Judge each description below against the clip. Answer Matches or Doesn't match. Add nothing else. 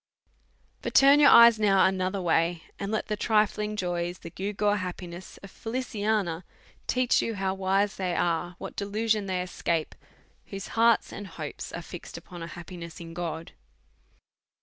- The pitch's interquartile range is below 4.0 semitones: Matches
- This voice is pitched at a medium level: Doesn't match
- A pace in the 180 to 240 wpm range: Doesn't match